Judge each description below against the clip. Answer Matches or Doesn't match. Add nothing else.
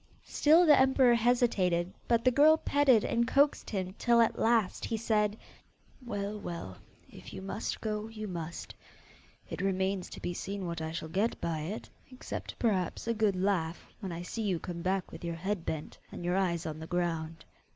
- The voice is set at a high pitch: Matches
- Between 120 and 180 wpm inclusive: Doesn't match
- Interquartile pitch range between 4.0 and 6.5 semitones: Matches